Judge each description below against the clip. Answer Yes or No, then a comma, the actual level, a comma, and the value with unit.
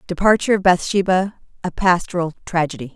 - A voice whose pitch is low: No, medium, 180 Hz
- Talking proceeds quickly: No, slow, 100 wpm